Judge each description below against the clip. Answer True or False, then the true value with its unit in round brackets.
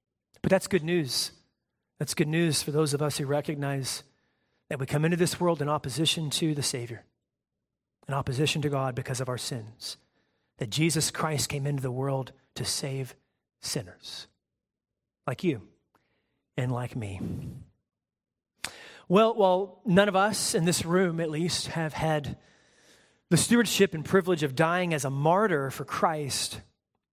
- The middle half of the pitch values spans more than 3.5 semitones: True (4.2 semitones)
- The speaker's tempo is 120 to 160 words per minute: True (155 wpm)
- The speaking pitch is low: False (150 Hz)